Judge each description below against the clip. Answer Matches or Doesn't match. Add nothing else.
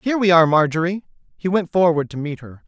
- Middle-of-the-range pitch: Matches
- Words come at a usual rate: Doesn't match